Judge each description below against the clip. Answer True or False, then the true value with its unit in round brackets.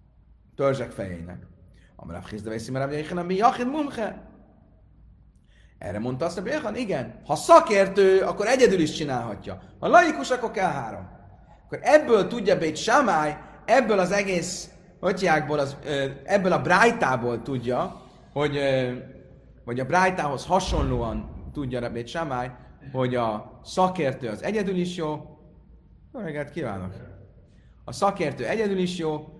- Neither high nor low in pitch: True (150 Hz)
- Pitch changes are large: True (7.0 semitones)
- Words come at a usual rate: True (115 wpm)